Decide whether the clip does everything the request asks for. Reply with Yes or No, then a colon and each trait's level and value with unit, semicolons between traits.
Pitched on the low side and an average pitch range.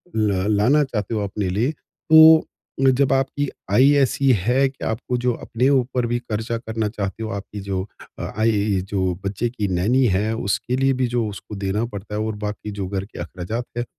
Yes: low, 110 Hz; average, 3.9 semitones